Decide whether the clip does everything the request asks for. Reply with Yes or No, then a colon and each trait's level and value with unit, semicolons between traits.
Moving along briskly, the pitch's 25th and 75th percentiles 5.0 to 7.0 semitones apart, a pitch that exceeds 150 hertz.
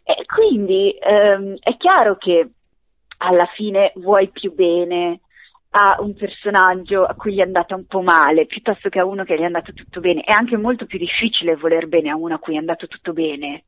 No: fast, 205 wpm; average, 3.3 semitones; medium, 185 Hz